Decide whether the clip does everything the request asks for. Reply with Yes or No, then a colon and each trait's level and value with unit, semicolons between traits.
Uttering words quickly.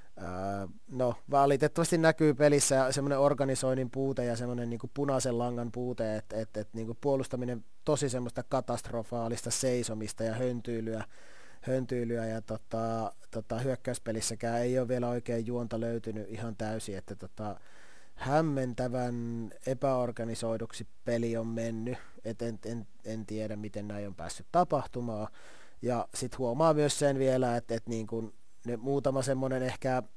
No: average, 130 wpm